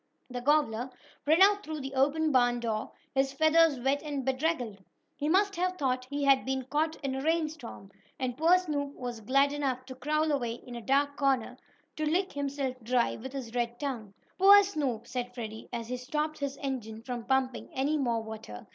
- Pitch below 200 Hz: No, very high, 270 Hz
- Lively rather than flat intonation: No, average, 3.7 semitones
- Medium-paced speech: Yes, average, 190 wpm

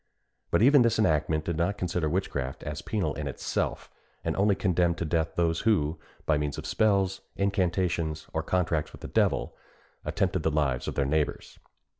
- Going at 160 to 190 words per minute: Yes, average, 175 wpm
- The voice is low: Yes, very low, 85 Hz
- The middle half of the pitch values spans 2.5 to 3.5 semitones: No, average, 4.0 semitones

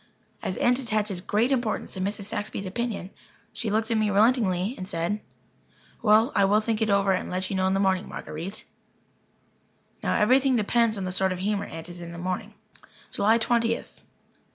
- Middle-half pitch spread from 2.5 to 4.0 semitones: Yes, average, 3.1 semitones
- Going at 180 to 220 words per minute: Yes, average, 190 wpm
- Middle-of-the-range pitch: No, high, 205 Hz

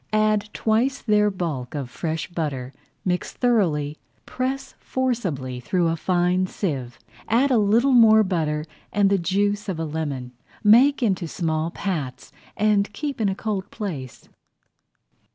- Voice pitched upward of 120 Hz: Yes, high, 190 Hz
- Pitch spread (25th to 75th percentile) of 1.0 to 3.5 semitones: No, wide, 5.6 semitones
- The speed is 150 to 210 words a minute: No, average, 140 wpm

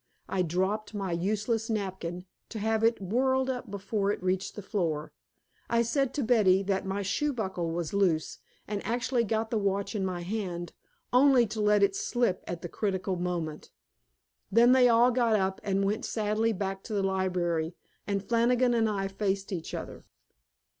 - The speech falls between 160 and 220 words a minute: Yes, average, 175 wpm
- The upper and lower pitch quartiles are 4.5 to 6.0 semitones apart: No, average, 3.4 semitones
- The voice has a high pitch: Yes, high, 200 Hz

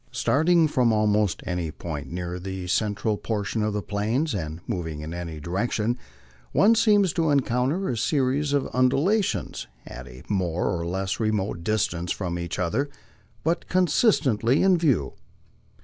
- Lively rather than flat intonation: Yes, wide, 8.1 semitones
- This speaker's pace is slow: No, average, 150 wpm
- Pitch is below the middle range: Yes, low, 105 Hz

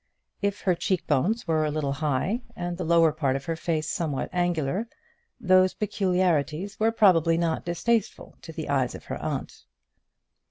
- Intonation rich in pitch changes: No, average, 3.3 semitones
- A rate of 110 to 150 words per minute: No, average, 165 wpm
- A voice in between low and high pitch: Yes, medium, 170 Hz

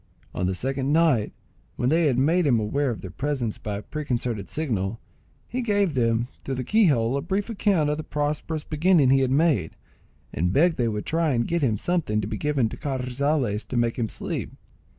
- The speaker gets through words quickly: Yes, fast, 210 wpm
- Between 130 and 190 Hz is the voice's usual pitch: Yes, low, 135 Hz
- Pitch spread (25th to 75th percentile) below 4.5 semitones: No, wide, 5.4 semitones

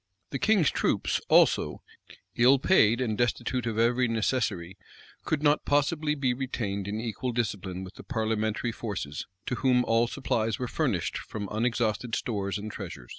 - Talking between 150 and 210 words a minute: Yes, average, 155 wpm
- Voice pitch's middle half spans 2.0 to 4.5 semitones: Yes, average, 3.4 semitones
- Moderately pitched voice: No, low, 115 Hz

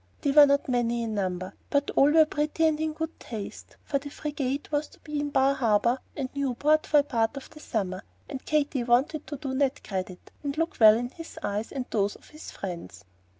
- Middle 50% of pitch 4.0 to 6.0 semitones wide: Yes, average, 4.8 semitones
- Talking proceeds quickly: Yes, fast, 220 wpm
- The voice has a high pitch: Yes, very high, 275 Hz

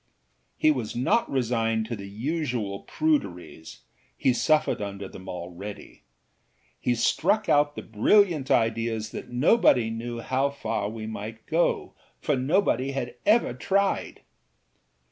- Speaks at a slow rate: Yes, slow, 125 wpm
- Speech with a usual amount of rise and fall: No, wide, 5.7 semitones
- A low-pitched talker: Yes, low, 120 Hz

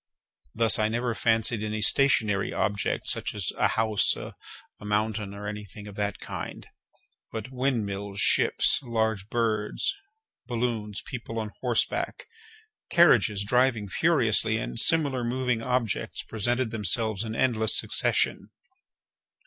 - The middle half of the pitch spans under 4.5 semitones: Yes, average, 2.7 semitones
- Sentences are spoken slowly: Yes, slow, 125 wpm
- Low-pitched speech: Yes, low, 110 Hz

